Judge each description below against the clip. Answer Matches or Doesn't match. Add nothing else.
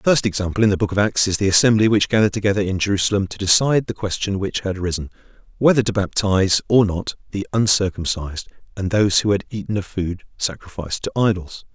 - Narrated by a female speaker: Doesn't match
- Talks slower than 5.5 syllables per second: Doesn't match